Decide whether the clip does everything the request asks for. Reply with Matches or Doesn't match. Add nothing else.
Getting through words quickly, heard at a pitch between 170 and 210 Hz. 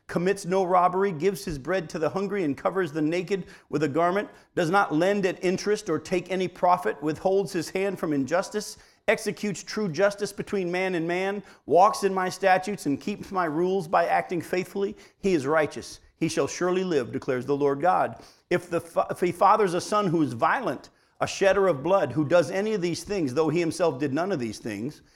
Matches